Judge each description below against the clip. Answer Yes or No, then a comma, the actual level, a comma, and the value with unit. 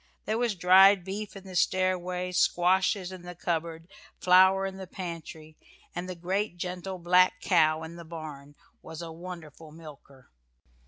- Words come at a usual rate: Yes, average, 155 wpm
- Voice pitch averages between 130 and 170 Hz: No, medium, 180 Hz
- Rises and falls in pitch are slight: Yes, narrow, 2.3 semitones